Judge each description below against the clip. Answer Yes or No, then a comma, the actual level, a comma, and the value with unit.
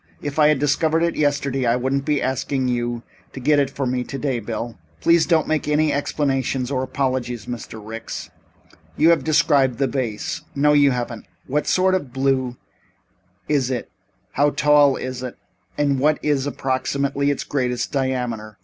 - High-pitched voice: No, low, 135 Hz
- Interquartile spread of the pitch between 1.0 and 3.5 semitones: Yes, average, 2.7 semitones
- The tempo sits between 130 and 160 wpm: No, average, 170 wpm